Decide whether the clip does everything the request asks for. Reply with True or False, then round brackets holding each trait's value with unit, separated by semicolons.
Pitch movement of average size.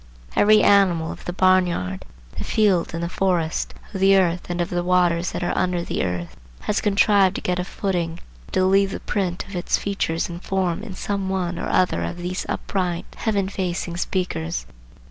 False (2.0 semitones)